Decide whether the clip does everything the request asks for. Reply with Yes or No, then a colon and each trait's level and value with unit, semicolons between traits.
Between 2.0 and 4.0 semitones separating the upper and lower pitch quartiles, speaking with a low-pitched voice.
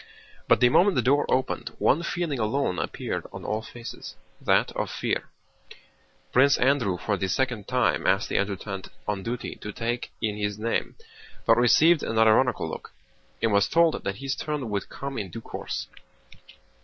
No: average, 4.8 semitones; low, 115 Hz